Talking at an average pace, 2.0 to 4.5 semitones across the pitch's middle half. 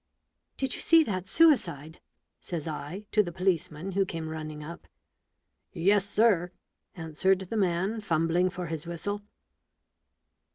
No: slow, 130 wpm; average, 3.8 semitones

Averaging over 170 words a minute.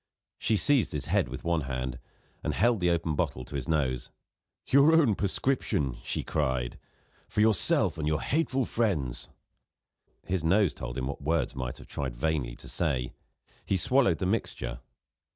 No: average, 165 wpm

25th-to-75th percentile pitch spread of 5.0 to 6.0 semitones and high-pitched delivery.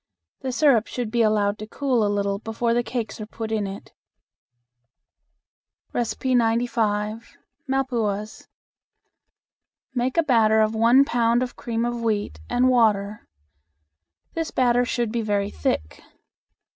No: narrow, 2.4 semitones; high, 230 Hz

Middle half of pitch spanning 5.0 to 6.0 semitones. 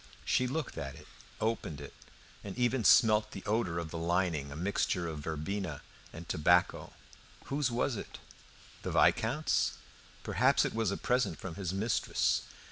Yes: wide, 5.6 semitones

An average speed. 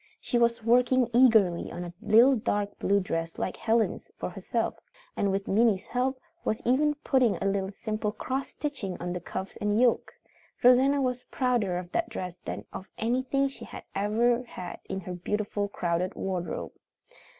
Yes: average, 170 wpm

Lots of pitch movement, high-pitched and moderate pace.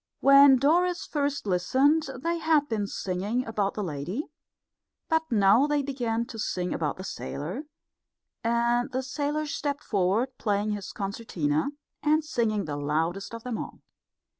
Yes: wide, 6.5 semitones; high, 235 Hz; average, 145 wpm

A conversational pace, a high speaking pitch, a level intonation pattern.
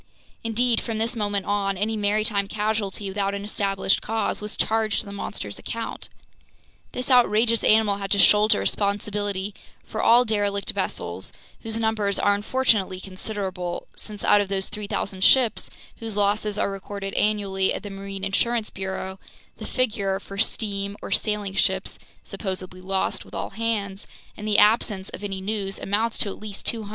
Yes: average, 165 wpm; high, 205 Hz; narrow, 1.8 semitones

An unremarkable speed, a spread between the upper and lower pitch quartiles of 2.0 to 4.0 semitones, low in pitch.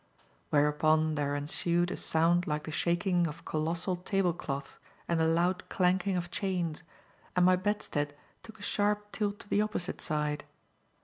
No: average, 160 wpm; average, 3.3 semitones; medium, 175 Hz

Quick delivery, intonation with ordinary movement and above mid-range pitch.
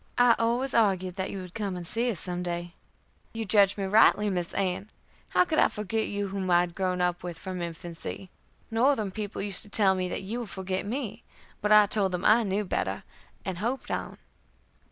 Yes: fast, 210 wpm; average, 3.0 semitones; high, 195 Hz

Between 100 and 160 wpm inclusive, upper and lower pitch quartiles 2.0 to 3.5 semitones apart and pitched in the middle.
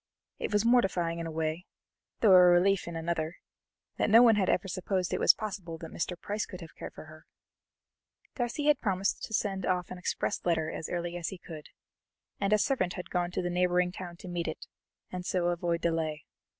No: fast, 205 wpm; narrow, 2.5 semitones; medium, 180 Hz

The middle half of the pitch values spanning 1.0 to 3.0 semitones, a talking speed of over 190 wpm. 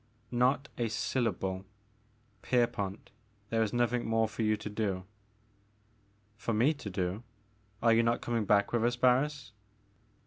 No: narrow, 2.6 semitones; average, 140 wpm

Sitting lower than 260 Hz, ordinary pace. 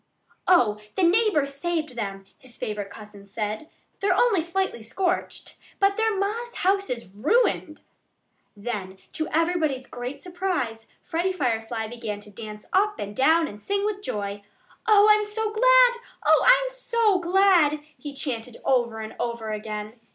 No: very high, 305 Hz; average, 150 wpm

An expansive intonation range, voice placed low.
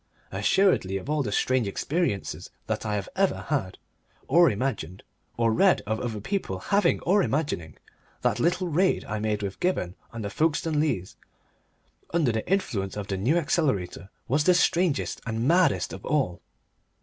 Yes: wide, 9.0 semitones; low, 130 Hz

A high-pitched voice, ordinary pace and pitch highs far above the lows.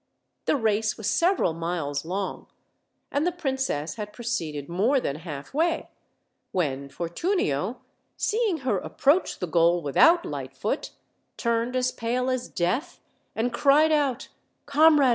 No: high, 235 Hz; slow, 130 wpm; wide, 8.8 semitones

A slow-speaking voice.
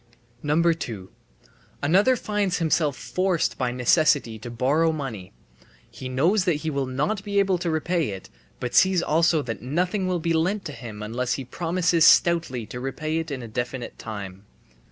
No: average, 170 wpm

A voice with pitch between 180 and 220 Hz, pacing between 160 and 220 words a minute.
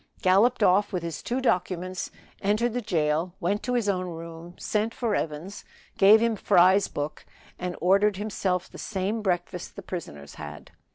Yes: high, 190 Hz; average, 165 wpm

